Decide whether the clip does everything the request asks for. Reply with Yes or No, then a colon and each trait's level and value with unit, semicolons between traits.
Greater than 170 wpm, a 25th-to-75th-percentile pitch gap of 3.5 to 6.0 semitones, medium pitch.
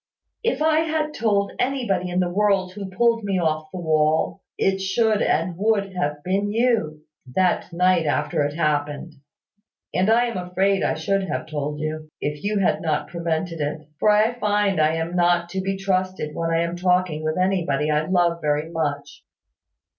Yes: average, 180 wpm; average, 4.1 semitones; medium, 180 Hz